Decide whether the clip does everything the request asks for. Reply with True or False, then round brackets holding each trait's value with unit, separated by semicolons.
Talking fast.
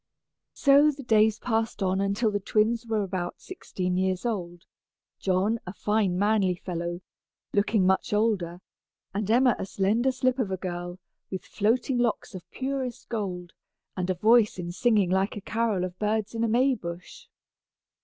False (160 wpm)